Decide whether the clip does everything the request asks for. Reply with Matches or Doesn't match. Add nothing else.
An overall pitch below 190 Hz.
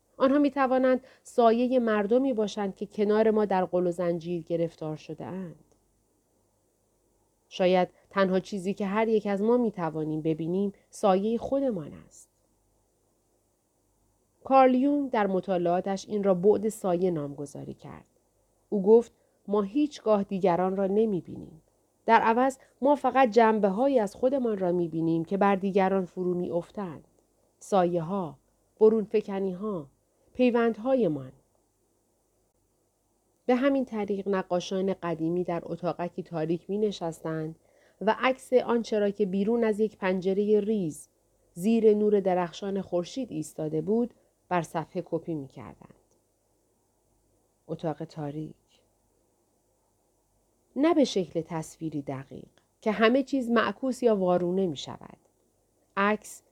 Doesn't match